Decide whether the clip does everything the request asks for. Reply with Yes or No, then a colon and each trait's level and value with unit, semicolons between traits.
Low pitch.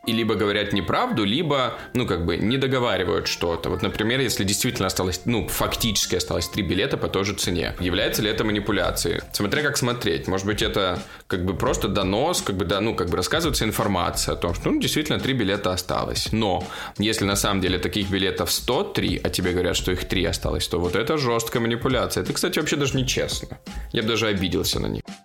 Yes: low, 105 Hz